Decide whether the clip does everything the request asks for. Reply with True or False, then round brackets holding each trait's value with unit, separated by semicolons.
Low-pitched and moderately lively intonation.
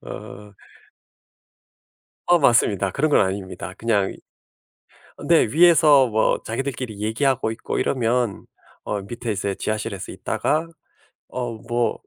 True (115 Hz; 4.5 semitones)